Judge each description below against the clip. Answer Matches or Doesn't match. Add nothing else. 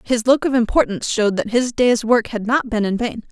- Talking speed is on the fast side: Matches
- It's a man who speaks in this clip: Doesn't match